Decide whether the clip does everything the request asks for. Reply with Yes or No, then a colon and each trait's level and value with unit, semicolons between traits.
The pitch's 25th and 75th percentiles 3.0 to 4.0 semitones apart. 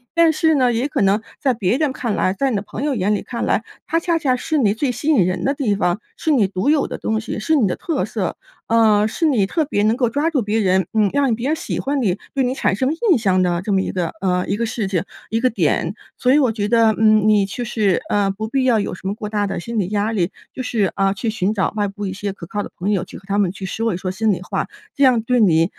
No: average, 4.6 semitones